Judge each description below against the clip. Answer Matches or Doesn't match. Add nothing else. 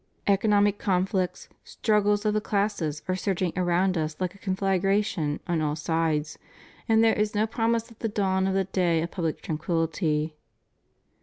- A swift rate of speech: Doesn't match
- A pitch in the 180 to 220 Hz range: Matches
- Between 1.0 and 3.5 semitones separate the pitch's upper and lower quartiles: Doesn't match